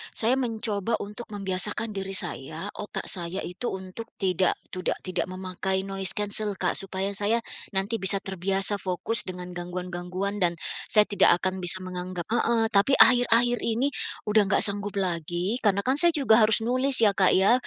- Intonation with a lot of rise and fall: No, average, 3.2 semitones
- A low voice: No, high, 195 Hz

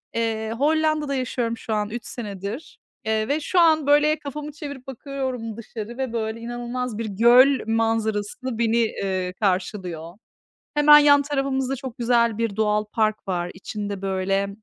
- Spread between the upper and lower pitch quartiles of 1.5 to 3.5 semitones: No, average, 4.3 semitones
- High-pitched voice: Yes, high, 230 Hz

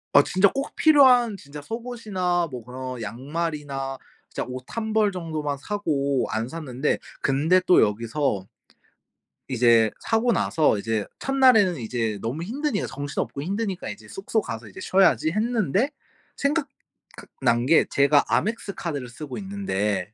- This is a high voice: No, medium, 155 Hz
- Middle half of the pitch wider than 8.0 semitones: Yes, wide, 8.7 semitones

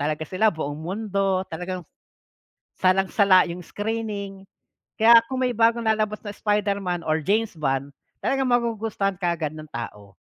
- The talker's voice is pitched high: Yes, high, 195 Hz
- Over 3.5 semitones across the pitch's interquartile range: Yes, average, 4.4 semitones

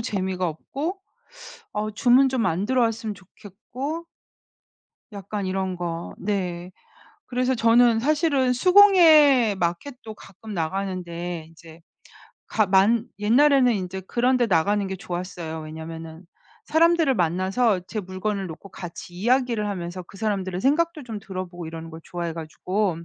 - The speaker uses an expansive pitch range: Yes, wide, 5.7 semitones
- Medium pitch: No, high, 200 Hz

